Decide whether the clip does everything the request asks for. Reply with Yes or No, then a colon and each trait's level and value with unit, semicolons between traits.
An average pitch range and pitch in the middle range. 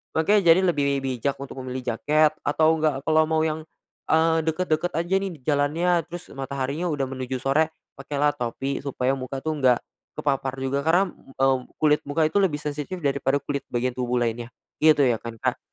Yes: average, 3.1 semitones; medium, 145 Hz